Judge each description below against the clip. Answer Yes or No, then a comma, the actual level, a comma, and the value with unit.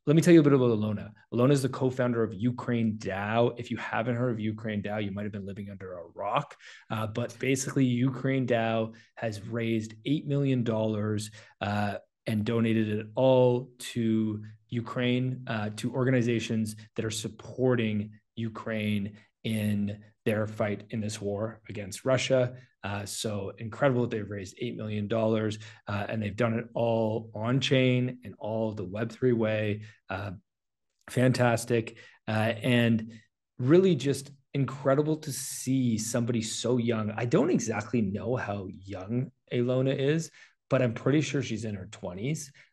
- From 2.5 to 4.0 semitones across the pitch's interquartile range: Yes, average, 2.8 semitones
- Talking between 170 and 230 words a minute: No, average, 155 wpm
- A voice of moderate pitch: No, low, 115 Hz